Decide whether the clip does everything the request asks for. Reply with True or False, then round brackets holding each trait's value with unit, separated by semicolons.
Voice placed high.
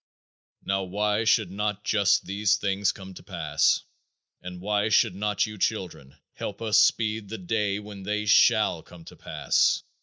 False (105 Hz)